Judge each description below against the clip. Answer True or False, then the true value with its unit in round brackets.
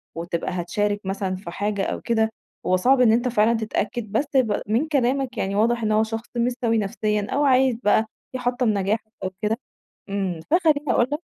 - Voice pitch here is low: False (220 Hz)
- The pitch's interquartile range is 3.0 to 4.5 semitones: True (3.4 semitones)